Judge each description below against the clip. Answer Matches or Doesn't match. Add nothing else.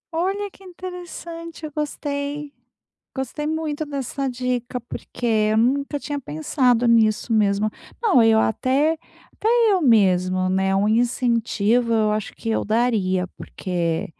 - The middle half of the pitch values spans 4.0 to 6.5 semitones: Matches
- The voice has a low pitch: Doesn't match